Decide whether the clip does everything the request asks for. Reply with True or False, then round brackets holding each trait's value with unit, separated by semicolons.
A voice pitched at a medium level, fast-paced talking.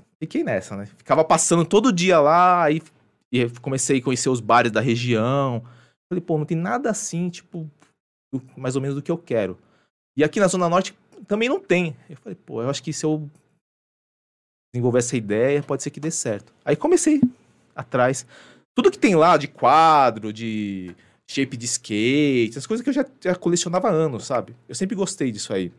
True (145 Hz; 195 wpm)